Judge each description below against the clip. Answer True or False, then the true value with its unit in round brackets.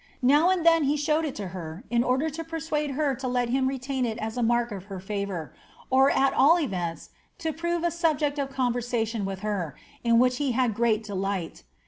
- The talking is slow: False (205 wpm)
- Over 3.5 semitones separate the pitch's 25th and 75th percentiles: True (5.6 semitones)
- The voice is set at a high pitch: True (250 Hz)